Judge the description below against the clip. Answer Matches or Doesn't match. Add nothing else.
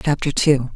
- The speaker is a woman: Matches